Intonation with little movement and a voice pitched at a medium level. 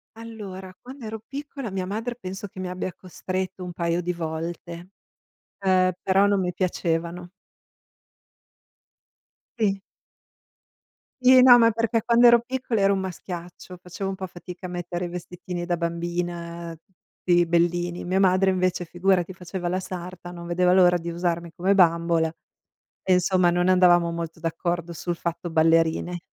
Yes: narrow, 1.8 semitones; medium, 180 Hz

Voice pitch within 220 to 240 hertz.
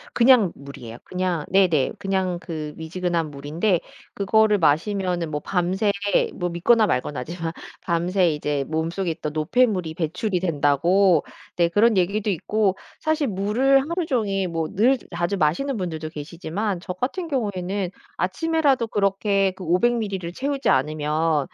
No: medium, 185 Hz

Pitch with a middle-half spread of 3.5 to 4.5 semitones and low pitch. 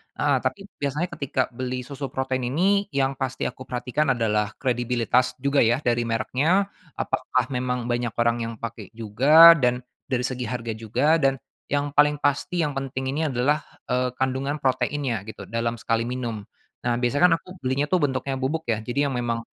No: average, 3.0 semitones; low, 130 Hz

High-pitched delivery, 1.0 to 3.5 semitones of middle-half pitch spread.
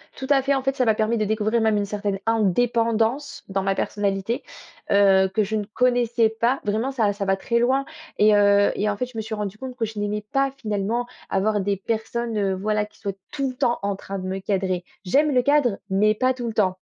Yes: high, 215 Hz; average, 3.1 semitones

